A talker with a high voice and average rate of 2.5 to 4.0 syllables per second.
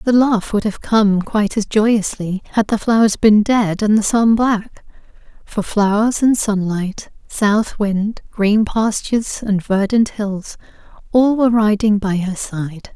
Yes: high, 210 Hz; 3.9 syllables/s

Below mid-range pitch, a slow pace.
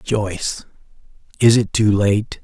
Yes: low, 105 Hz; slow, 125 wpm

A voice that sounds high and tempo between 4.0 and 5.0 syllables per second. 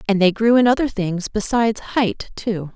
Yes: high, 210 Hz; 4.7 syllables/s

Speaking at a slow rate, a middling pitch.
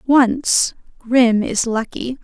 No: slow, 105 wpm; high, 240 Hz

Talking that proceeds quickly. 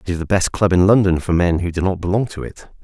Yes: fast, 315 wpm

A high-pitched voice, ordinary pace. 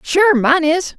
Yes: very high, 320 Hz; average, 185 wpm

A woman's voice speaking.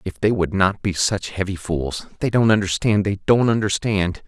No: male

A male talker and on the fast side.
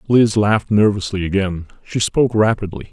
No: male; average, 145 wpm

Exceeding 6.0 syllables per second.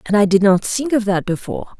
Yes: 6.3 syllables/s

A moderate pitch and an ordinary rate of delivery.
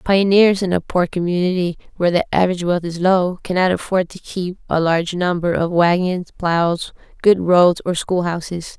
Yes: medium, 180 Hz; average, 175 wpm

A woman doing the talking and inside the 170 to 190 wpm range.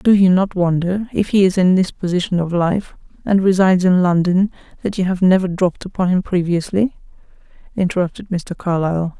Yes: female; average, 175 wpm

